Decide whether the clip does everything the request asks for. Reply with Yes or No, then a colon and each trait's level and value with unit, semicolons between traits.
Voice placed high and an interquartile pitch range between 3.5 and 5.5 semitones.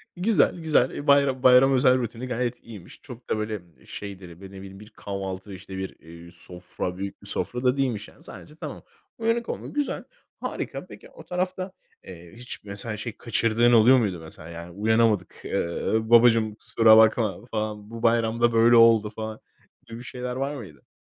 No: low, 115 Hz; average, 4.1 semitones